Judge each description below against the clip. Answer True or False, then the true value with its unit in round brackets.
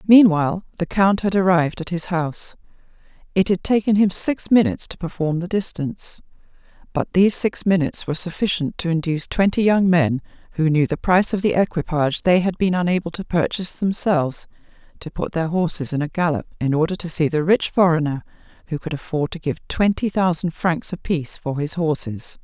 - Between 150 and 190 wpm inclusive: True (185 wpm)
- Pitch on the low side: False (170 Hz)